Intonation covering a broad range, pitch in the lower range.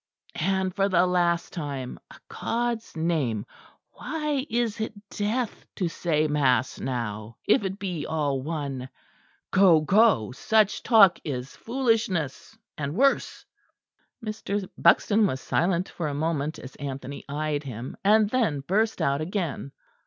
No: wide, 6.9 semitones; medium, 170 Hz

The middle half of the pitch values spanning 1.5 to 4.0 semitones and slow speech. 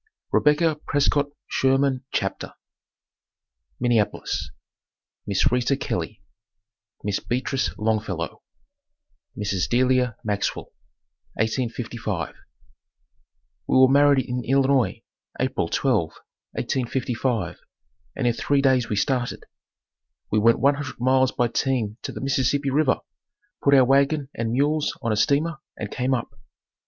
Yes: average, 3.6 semitones; slow, 115 wpm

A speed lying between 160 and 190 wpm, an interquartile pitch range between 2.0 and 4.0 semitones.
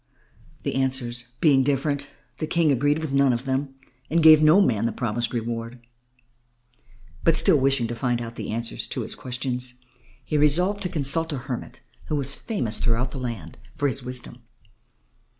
Yes: average, 170 wpm; average, 3.7 semitones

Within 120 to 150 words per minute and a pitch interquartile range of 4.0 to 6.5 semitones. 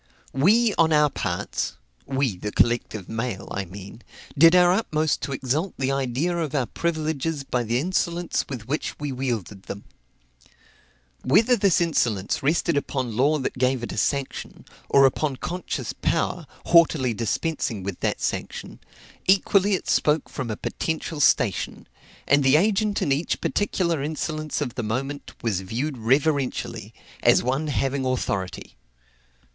Yes: average, 145 wpm; average, 4.9 semitones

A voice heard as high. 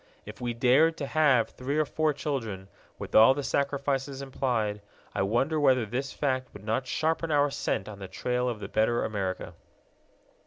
No: low, 130 Hz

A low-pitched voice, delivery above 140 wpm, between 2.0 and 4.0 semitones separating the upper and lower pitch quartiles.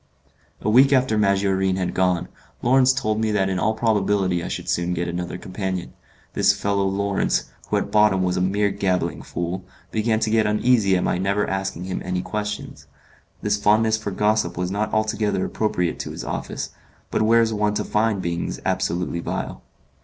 Yes: low, 100 Hz; average, 185 wpm; average, 2.8 semitones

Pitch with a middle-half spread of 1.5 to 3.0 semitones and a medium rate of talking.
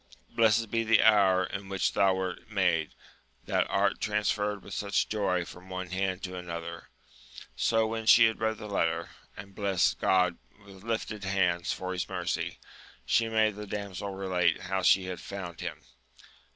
Yes: narrow, 2.4 semitones; average, 165 wpm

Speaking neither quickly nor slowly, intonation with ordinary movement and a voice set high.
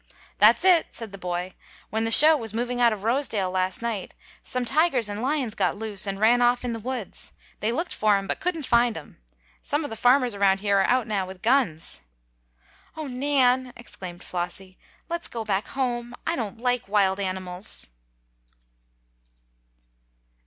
Yes: average, 175 wpm; average, 4.3 semitones; high, 225 Hz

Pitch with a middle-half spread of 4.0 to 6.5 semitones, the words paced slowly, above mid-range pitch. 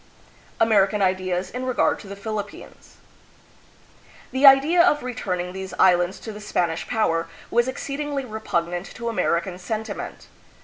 Yes: wide, 5.4 semitones; slow, 130 wpm; high, 210 Hz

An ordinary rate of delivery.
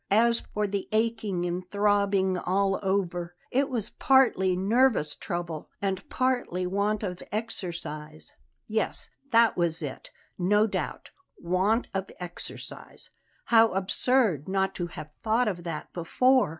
No: slow, 130 wpm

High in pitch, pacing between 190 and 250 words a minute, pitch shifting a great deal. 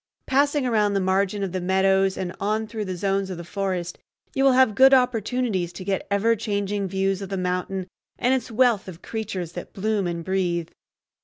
No: high, 195 Hz; average, 200 wpm; average, 3.0 semitones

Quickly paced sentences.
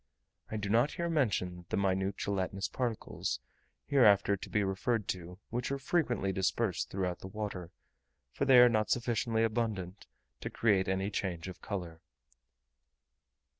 No: average, 145 wpm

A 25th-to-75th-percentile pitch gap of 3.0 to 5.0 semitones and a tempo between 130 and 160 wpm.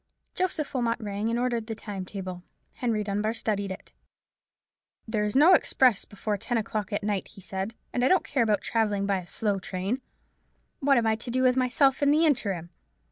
No: average, 3.9 semitones; average, 195 wpm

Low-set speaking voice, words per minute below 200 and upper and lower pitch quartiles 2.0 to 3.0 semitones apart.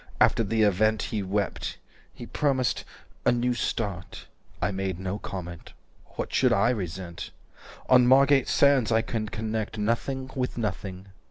No: low, 110 Hz; average, 150 wpm; average, 4.1 semitones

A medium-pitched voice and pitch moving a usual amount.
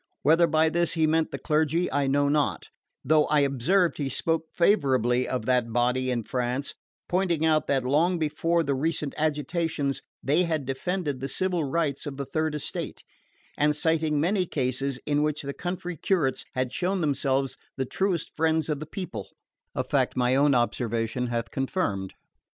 Yes: medium, 150 Hz; average, 3.6 semitones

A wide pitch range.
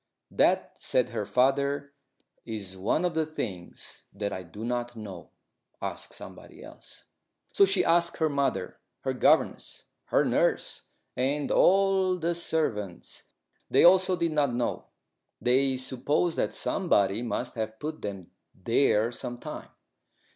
Yes: wide, 6.6 semitones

